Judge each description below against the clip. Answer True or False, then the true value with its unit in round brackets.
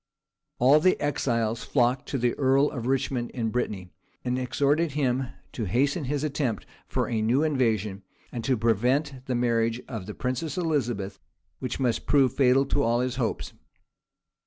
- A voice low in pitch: True (125 Hz)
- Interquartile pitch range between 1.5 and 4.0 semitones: True (3.1 semitones)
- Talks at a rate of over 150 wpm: True (160 wpm)